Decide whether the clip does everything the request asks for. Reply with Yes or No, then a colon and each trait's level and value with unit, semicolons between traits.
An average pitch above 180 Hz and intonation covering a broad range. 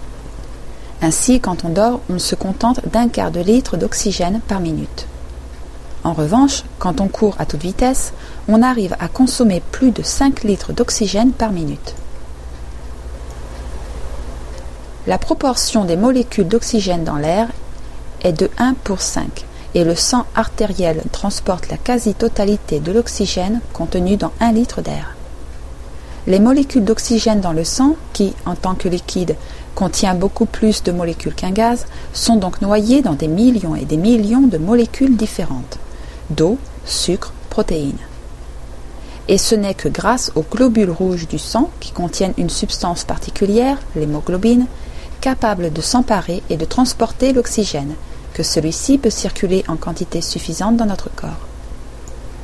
Yes: high, 190 Hz; wide, 7.9 semitones